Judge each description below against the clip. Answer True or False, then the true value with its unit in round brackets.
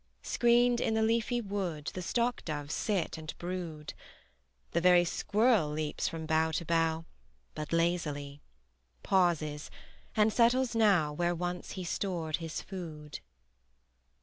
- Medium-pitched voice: True (175 Hz)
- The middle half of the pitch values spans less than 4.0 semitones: False (4.9 semitones)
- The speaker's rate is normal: False (130 wpm)